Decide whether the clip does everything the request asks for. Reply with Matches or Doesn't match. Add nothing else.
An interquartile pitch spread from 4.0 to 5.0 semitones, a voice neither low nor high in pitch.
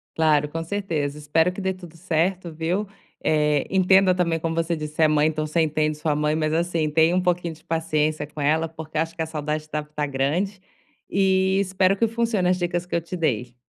Doesn't match